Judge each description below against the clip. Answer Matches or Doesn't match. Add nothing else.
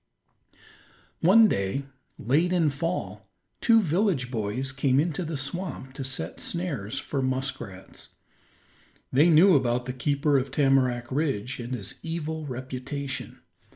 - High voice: Doesn't match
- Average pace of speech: Doesn't match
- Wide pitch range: Doesn't match